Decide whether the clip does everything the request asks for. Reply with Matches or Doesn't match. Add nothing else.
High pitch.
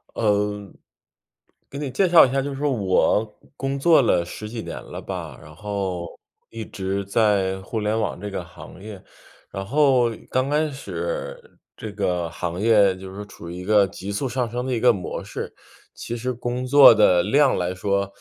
Doesn't match